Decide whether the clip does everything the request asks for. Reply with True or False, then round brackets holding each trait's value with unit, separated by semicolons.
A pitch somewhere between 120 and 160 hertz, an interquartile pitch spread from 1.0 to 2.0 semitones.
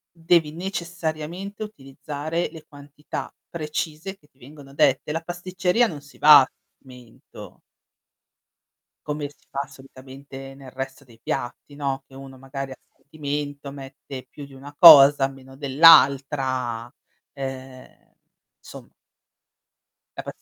False (140 Hz; 2.6 semitones)